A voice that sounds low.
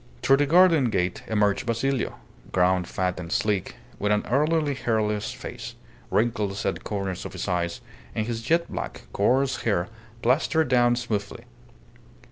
Yes: low, 110 Hz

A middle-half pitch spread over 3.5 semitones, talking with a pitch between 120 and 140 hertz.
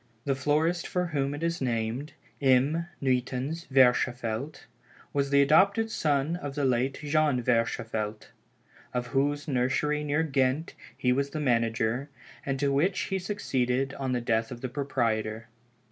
No: average, 3.2 semitones; low, 135 Hz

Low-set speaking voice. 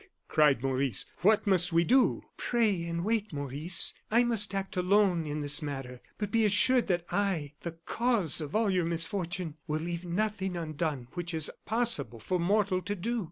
No: medium, 175 Hz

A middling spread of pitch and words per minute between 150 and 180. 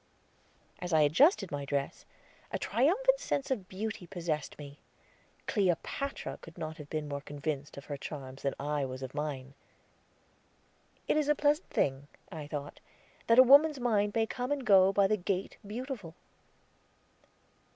No: wide, 9.0 semitones; average, 155 wpm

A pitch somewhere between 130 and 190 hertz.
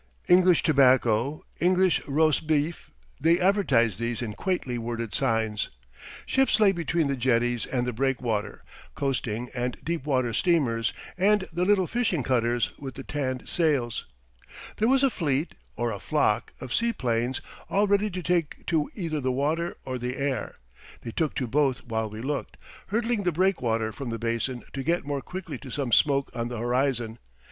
Yes: low, 135 Hz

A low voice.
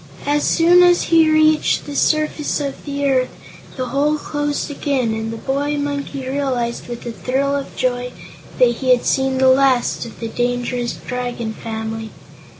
No: very high, 265 Hz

